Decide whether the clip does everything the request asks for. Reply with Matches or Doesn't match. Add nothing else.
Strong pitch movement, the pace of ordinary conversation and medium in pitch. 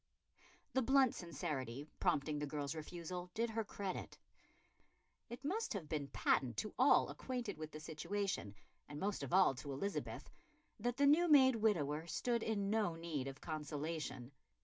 Matches